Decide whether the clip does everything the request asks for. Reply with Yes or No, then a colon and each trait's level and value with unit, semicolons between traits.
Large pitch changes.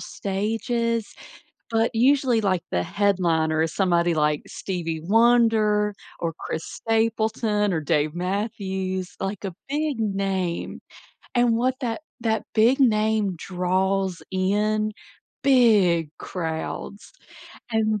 No: average, 3.8 semitones